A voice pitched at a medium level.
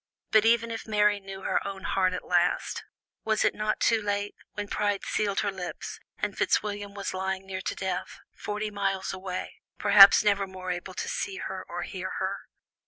No: high, 200 Hz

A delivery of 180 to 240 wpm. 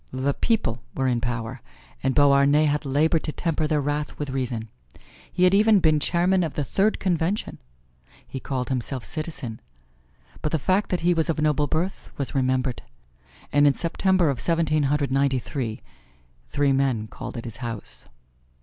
No: average, 170 wpm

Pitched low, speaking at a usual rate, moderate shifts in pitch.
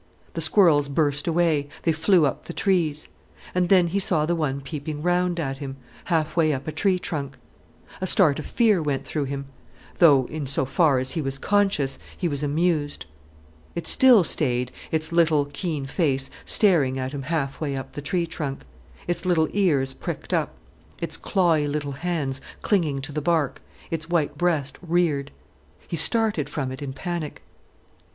No: medium, 155 Hz; average, 170 wpm; average, 3.8 semitones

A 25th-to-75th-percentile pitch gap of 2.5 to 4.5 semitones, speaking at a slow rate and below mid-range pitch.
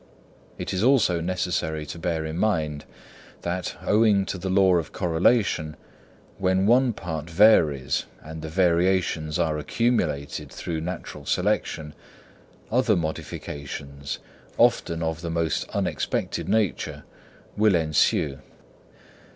Yes: average, 3.5 semitones; slow, 115 wpm; very low, 85 Hz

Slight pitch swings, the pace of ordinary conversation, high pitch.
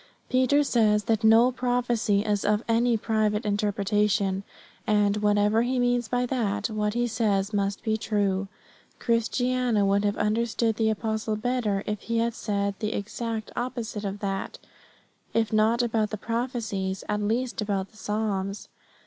Yes: narrow, 2.2 semitones; average, 155 wpm; high, 215 Hz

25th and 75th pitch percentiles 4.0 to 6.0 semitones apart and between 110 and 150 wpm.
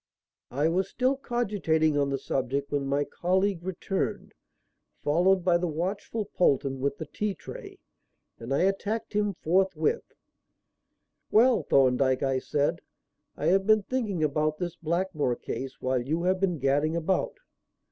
Yes: wide, 5.5 semitones; average, 145 wpm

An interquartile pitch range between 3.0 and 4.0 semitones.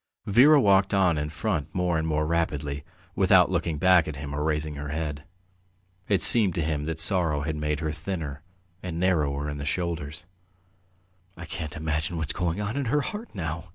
Yes: average, 3.5 semitones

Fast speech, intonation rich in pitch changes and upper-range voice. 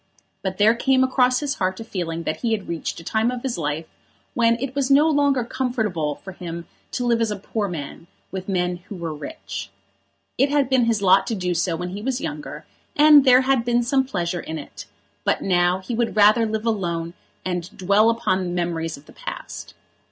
Yes: fast, 210 wpm; wide, 5.9 semitones; high, 205 Hz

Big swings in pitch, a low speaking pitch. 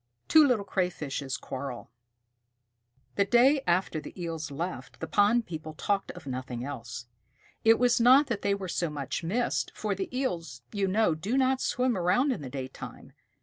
No: wide, 8.1 semitones; medium, 185 Hz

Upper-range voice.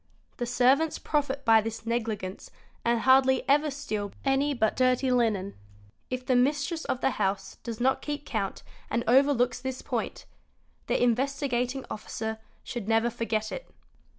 Yes: very high, 250 Hz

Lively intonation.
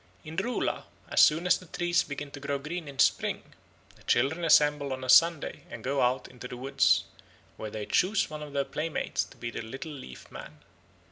No: average, 3.6 semitones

